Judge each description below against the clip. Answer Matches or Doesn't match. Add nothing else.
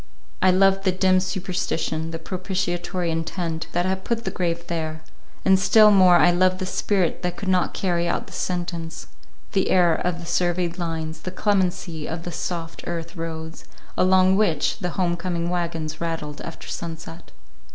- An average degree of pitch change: Doesn't match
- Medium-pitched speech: Matches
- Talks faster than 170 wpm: Doesn't match